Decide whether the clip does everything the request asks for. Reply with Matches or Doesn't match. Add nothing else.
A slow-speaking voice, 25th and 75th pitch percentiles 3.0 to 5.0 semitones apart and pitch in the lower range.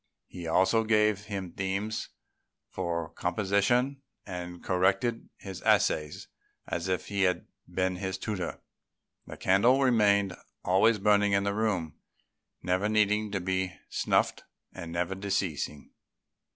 Doesn't match